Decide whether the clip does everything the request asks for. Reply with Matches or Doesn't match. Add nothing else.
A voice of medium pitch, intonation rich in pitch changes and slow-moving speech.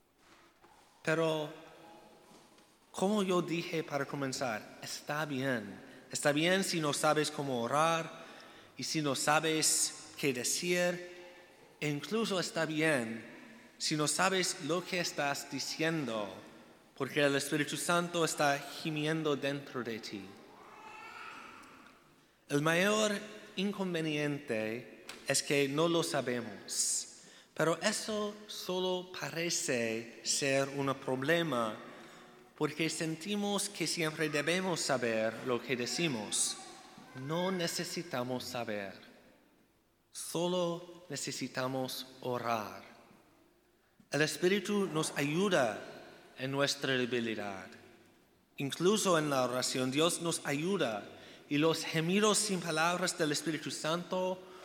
Doesn't match